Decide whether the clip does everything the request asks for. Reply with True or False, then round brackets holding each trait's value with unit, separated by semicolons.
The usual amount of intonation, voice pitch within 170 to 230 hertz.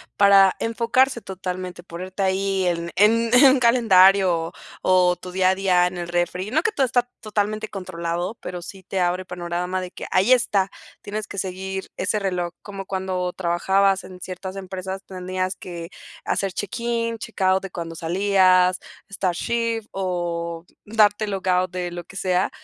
False (2.2 semitones; 190 Hz)